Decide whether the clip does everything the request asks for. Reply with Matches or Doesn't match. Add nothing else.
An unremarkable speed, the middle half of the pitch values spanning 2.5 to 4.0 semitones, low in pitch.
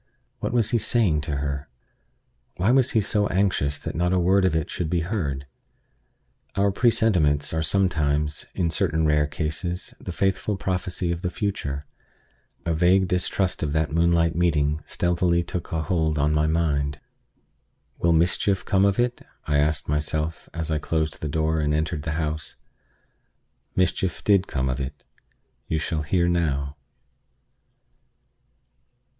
Matches